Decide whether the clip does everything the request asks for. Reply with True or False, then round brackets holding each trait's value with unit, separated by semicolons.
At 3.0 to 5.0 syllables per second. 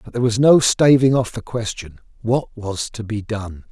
True (4.9 syllables/s)